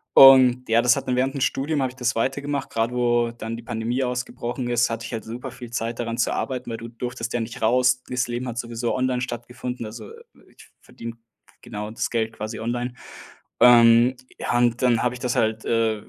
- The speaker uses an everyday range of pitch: No, narrow, 1.5 semitones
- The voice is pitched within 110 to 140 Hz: Yes, low, 120 Hz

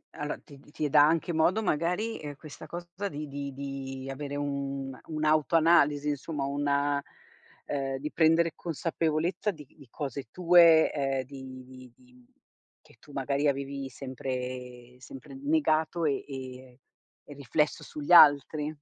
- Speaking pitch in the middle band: Yes, medium, 145 Hz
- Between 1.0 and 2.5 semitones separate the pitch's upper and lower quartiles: No, average, 2.9 semitones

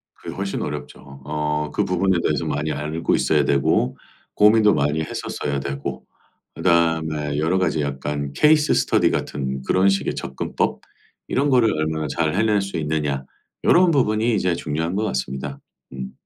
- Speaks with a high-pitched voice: No, very low, 80 Hz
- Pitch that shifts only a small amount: No, average, 5.2 semitones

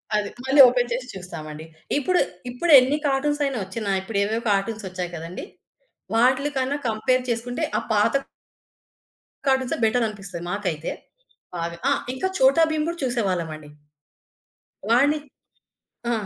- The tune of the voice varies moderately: No, wide, 5.8 semitones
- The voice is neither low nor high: No, high, 230 Hz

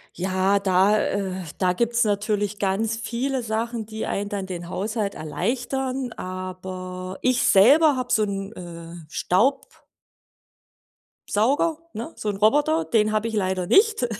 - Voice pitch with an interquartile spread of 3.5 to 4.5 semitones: Yes, average, 4.0 semitones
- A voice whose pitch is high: Yes, high, 210 Hz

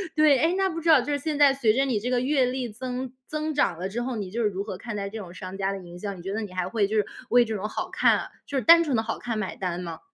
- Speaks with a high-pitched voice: Yes, high, 230 Hz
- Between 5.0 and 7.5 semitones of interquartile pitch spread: Yes, wide, 5.5 semitones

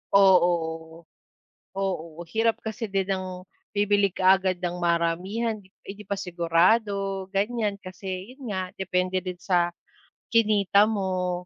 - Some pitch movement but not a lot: No, narrow, 2.2 semitones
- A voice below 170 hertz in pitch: No, high, 190 Hz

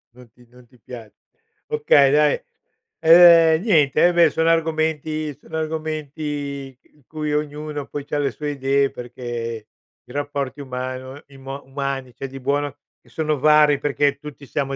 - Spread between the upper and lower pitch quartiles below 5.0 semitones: Yes, narrow, 2.4 semitones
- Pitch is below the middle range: No, medium, 145 Hz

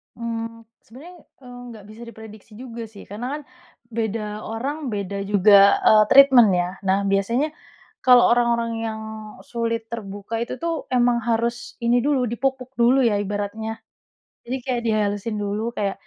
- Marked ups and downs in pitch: No, average, 2.7 semitones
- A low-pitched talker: No, high, 230 Hz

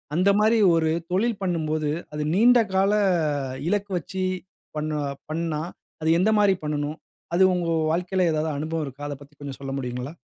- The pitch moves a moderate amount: Yes, average, 4.0 semitones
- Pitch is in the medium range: Yes, medium, 165 Hz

